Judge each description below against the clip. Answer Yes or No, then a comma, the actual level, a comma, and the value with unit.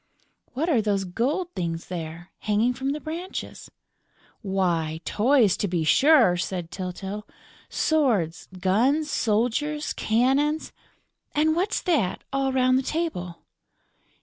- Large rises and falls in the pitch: Yes, wide, 8.3 semitones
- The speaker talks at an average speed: No, slow, 120 wpm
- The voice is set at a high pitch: Yes, high, 230 Hz